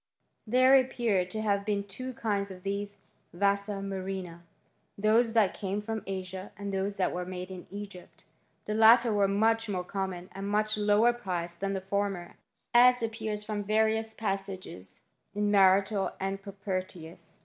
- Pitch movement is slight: Yes, narrow, 2.3 semitones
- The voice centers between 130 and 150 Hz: No, high, 200 Hz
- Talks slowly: No, average, 160 wpm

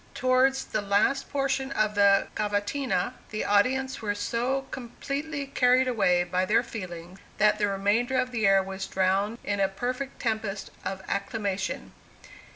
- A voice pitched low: No, high, 215 Hz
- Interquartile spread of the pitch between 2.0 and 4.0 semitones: No, average, 4.5 semitones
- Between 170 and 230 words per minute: No, average, 150 wpm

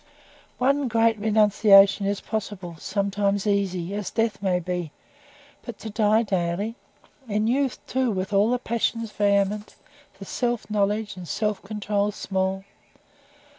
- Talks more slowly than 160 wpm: Yes, slow, 135 wpm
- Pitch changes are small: Yes, narrow, 2.2 semitones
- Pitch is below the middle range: No, high, 205 Hz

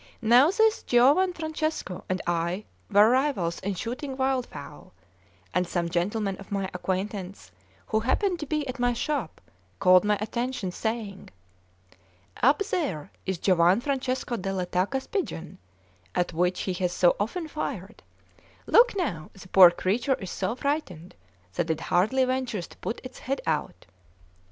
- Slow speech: No, average, 145 wpm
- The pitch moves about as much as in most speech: No, wide, 6.6 semitones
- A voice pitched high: Yes, high, 210 Hz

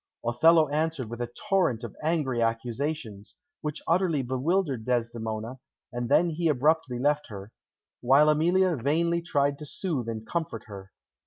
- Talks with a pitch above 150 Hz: No, medium, 140 Hz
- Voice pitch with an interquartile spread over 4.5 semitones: Yes, wide, 5.5 semitones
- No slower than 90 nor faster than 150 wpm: Yes, average, 145 wpm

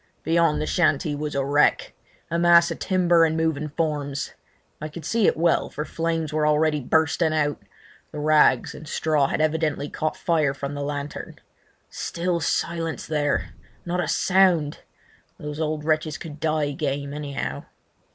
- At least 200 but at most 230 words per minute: No, average, 155 wpm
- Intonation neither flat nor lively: No, narrow, 2.0 semitones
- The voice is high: No, medium, 155 Hz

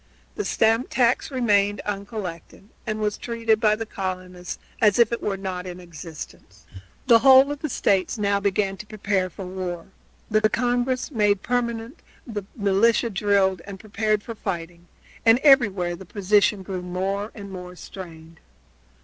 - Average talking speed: Yes, average, 160 wpm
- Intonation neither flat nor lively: Yes, average, 3.4 semitones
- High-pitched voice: Yes, high, 205 Hz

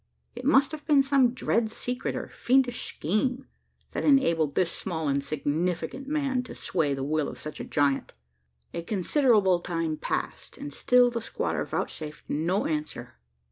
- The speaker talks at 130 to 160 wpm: Yes, average, 155 wpm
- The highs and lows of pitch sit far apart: Yes, wide, 8.6 semitones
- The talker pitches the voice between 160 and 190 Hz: Yes, medium, 185 Hz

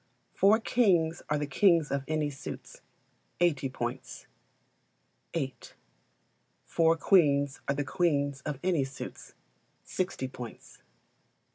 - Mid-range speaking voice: Yes, medium, 150 Hz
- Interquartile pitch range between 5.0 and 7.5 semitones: No, average, 3.8 semitones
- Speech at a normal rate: No, slow, 110 wpm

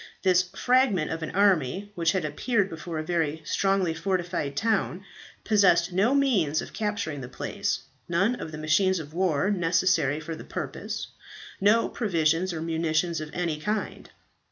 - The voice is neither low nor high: Yes, medium, 175 Hz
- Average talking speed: Yes, average, 155 wpm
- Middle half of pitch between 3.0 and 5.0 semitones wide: Yes, average, 3.9 semitones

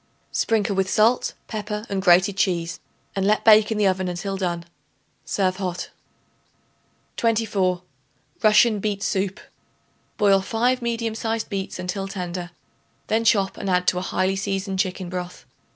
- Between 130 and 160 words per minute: Yes, average, 145 wpm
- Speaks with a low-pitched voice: No, high, 195 Hz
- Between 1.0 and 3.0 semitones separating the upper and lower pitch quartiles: Yes, narrow, 2.5 semitones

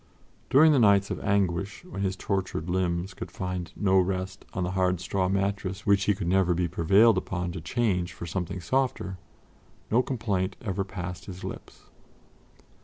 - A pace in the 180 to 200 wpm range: No, average, 170 wpm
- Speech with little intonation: Yes, narrow, 1.8 semitones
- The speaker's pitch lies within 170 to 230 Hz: No, very low, 95 Hz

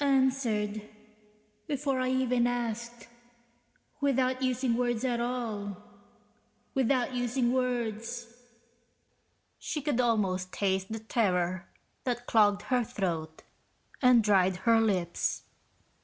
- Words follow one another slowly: Yes, slow, 100 wpm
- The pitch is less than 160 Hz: No, high, 235 Hz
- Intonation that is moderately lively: Yes, average, 3.4 semitones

